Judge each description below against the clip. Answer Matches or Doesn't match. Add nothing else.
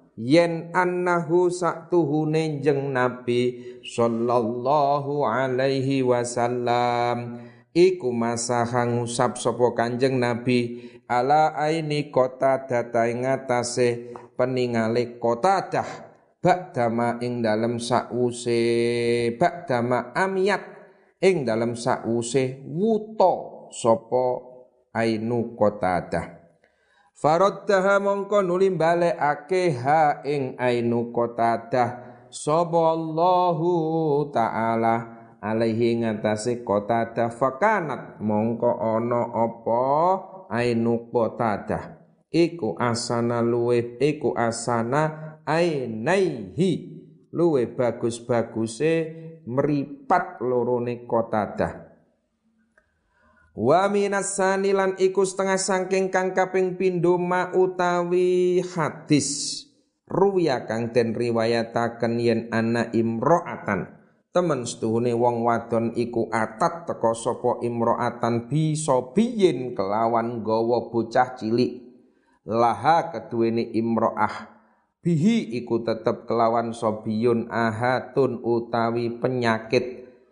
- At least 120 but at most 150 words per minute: Doesn't match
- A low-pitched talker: Matches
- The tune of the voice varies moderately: Doesn't match